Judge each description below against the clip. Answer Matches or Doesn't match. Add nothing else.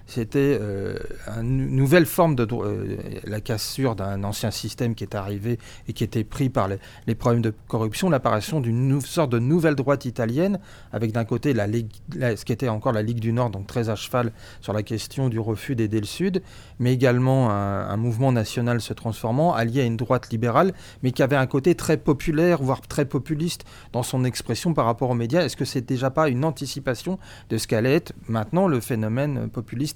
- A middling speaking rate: Matches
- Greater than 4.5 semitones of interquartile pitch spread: Doesn't match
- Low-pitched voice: Matches